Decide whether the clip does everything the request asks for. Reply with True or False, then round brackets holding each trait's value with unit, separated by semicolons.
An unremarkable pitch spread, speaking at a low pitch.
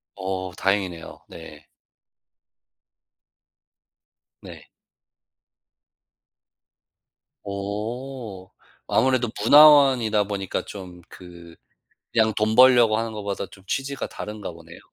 True (4.2 semitones; 105 Hz)